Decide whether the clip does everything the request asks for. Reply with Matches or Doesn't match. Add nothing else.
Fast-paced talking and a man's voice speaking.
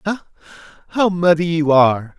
Doesn't match